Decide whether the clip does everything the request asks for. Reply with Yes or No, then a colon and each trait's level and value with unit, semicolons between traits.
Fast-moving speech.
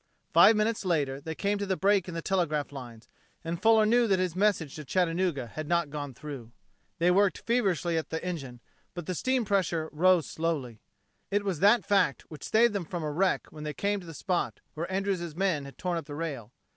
Yes: fast, 215 wpm